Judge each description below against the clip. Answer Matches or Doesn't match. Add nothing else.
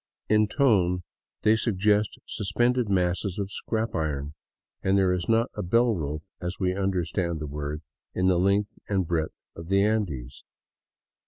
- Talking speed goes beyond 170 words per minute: Doesn't match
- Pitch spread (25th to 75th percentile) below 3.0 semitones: Doesn't match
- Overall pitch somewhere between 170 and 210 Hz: Doesn't match